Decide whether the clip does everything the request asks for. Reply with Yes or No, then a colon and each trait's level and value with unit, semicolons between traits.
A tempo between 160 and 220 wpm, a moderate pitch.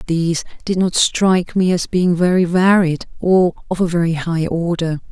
Yes: average, 175 wpm; medium, 175 Hz